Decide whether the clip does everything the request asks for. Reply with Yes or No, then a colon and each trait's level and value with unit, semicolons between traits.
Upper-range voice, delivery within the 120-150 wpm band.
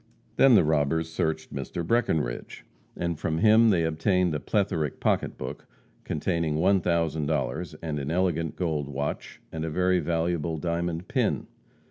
No: very low, 80 Hz; average, 145 wpm